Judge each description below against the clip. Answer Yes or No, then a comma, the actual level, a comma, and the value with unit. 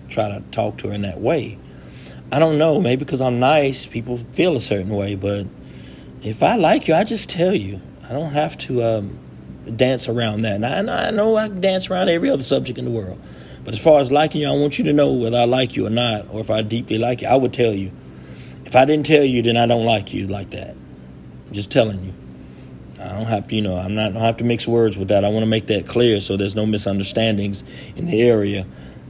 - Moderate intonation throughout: Yes, average, 4.8 semitones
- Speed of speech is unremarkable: No, fast, 250 wpm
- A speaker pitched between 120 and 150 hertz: No, low, 110 Hz